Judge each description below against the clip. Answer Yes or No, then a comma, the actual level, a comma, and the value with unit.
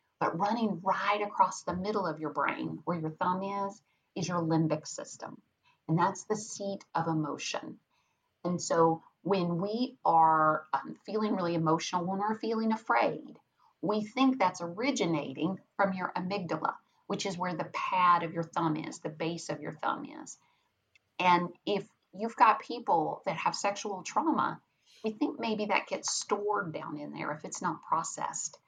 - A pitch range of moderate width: Yes, average, 3.8 semitones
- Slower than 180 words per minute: Yes, average, 165 wpm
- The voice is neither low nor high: Yes, medium, 180 Hz